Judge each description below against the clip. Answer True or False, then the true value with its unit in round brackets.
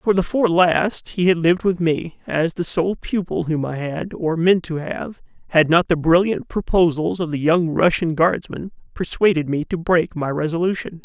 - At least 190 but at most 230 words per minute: True (195 wpm)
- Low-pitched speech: False (170 Hz)